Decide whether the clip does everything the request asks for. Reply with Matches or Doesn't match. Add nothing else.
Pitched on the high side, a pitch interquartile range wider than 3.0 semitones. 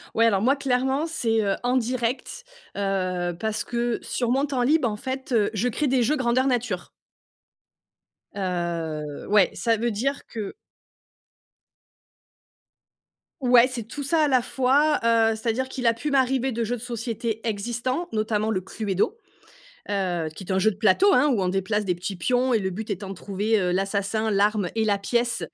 Matches